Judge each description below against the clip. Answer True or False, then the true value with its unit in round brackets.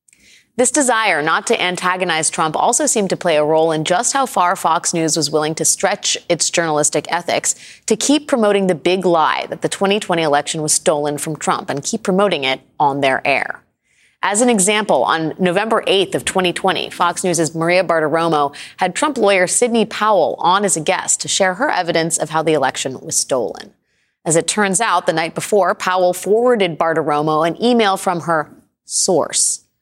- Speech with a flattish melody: False (4.2 semitones)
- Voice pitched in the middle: True (180 Hz)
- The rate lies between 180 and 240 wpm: True (185 wpm)